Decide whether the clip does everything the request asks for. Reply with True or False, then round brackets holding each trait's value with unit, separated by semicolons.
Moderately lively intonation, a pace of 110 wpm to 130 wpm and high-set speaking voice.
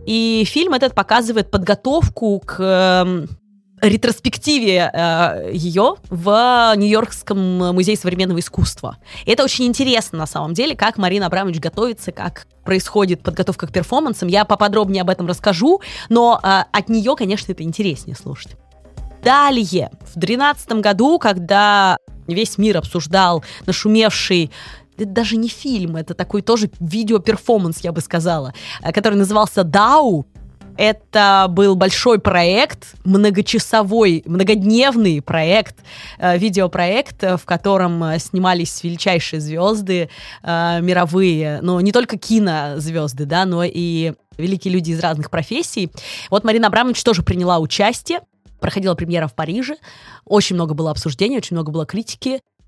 True (4.0 semitones; 125 wpm; 195 Hz)